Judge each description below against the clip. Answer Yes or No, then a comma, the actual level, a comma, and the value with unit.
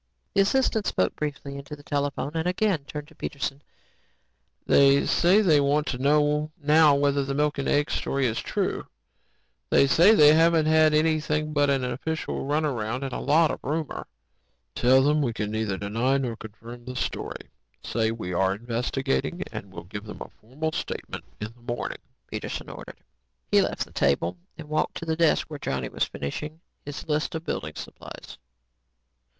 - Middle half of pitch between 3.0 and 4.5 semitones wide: Yes, average, 4.2 semitones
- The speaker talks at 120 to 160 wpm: No, average, 170 wpm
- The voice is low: No, medium, 145 Hz